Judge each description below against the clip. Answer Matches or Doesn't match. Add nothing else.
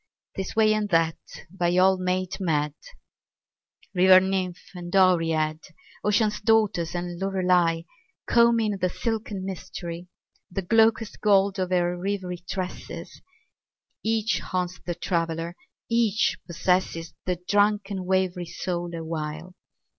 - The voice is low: Doesn't match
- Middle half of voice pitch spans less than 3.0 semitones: Matches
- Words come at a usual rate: Doesn't match